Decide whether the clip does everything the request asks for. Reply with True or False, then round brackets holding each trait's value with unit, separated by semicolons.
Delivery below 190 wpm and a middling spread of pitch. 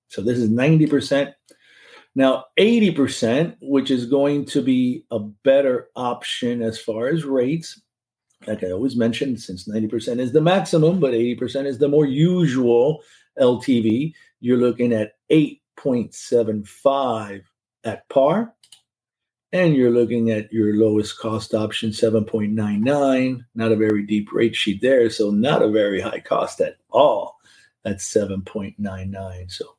True (160 wpm; 4.3 semitones)